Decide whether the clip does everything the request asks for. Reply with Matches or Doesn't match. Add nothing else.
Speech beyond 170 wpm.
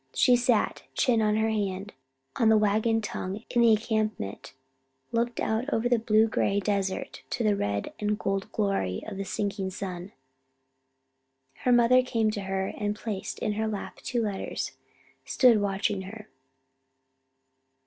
Doesn't match